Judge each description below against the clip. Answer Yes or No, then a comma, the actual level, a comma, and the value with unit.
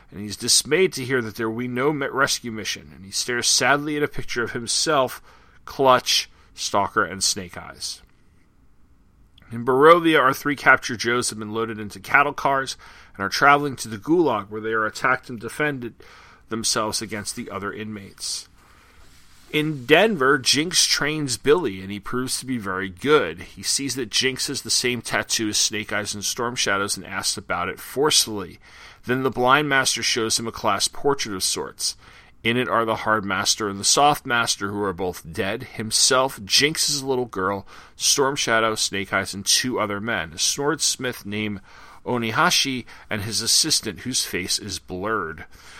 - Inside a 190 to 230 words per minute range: No, average, 175 wpm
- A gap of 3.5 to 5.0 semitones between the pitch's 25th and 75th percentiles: Yes, average, 4.4 semitones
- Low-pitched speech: Yes, low, 115 Hz